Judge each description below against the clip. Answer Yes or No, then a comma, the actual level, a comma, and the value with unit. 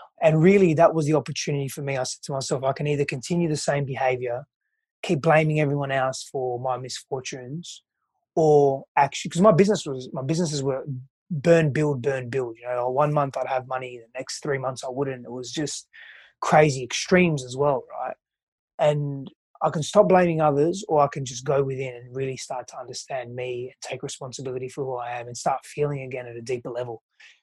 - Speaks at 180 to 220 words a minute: Yes, fast, 205 wpm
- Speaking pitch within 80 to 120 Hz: No, medium, 140 Hz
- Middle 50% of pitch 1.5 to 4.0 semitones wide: Yes, average, 3.1 semitones